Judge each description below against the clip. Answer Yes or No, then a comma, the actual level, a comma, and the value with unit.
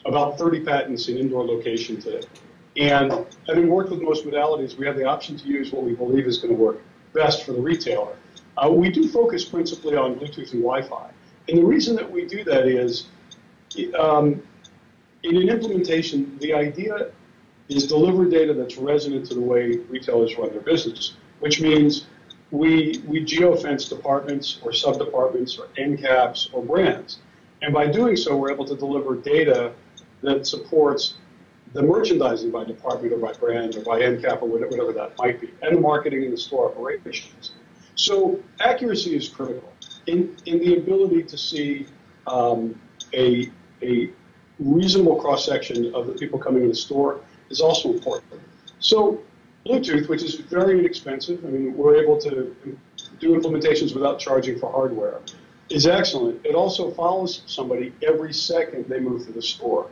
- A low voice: No, medium, 155 Hz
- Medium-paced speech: Yes, average, 165 wpm